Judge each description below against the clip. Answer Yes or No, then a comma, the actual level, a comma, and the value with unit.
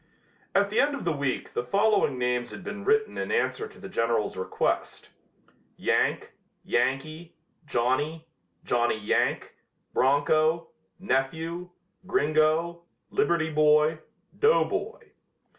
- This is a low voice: No, medium, 155 Hz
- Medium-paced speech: No, slow, 110 wpm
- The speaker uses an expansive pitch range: Yes, wide, 6.3 semitones